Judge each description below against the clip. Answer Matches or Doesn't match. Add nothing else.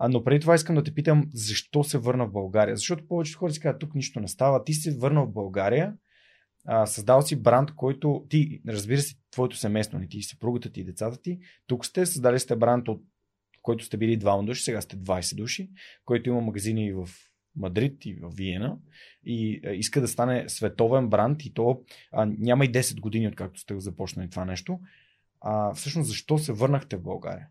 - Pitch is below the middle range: Matches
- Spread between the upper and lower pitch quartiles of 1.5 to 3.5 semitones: Doesn't match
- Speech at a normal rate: Doesn't match